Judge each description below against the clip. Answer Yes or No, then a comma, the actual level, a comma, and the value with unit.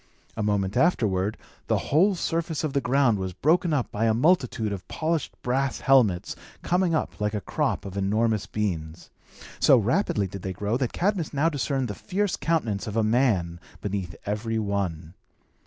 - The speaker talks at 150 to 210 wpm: Yes, average, 170 wpm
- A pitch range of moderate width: No, wide, 6.7 semitones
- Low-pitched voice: Yes, low, 110 Hz